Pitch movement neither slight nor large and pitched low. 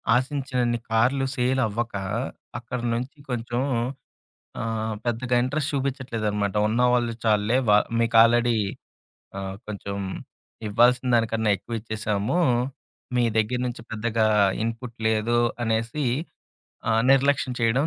No: narrow, 2.1 semitones; low, 120 Hz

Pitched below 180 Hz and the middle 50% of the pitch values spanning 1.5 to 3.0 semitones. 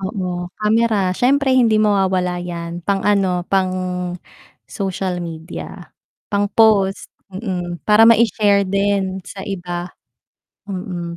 No: high, 195 Hz; average, 2.7 semitones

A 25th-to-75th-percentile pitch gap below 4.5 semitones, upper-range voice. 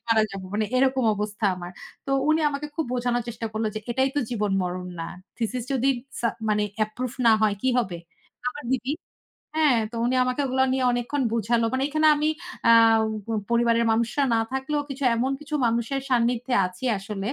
Yes: average, 3.3 semitones; high, 240 Hz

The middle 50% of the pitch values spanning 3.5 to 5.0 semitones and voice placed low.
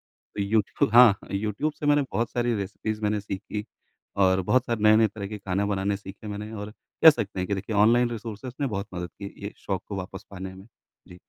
No: narrow, 2.4 semitones; low, 105 Hz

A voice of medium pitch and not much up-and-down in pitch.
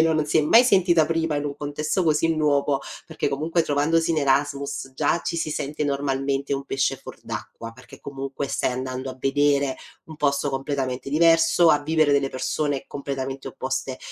Yes: medium, 145 Hz; narrow, 2.3 semitones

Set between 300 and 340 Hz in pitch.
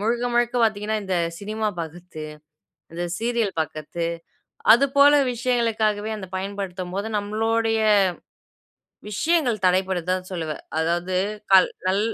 No: high, 205 Hz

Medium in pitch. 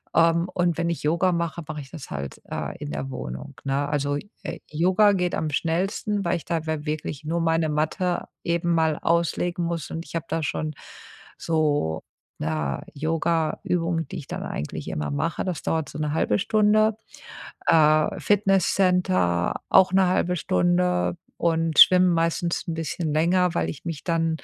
Yes: medium, 165 Hz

